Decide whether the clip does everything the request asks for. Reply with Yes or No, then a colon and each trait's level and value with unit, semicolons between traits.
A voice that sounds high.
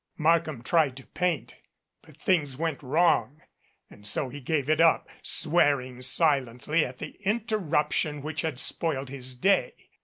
No: medium, 150 Hz